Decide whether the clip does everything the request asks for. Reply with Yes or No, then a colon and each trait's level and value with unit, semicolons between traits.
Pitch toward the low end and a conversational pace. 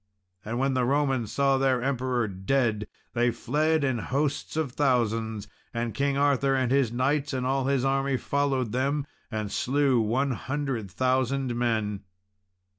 Yes: low, 130 Hz; average, 150 wpm